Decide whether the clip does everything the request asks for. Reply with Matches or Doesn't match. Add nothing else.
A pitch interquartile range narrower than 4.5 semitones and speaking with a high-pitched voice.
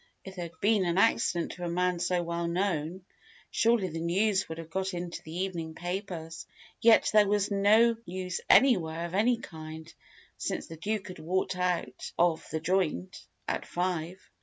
Doesn't match